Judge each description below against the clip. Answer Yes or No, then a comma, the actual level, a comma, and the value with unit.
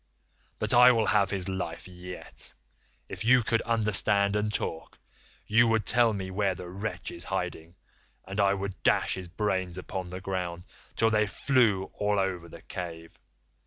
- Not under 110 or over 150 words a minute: No, average, 165 wpm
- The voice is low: Yes, low, 100 Hz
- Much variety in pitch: No, average, 2.8 semitones